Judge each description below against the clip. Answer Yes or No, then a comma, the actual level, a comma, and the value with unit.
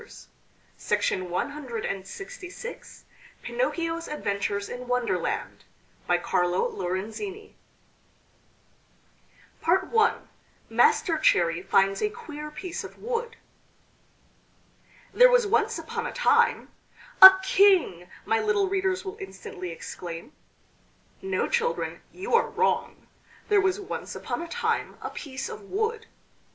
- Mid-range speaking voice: No, very high, 375 Hz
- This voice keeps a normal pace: No, slow, 105 wpm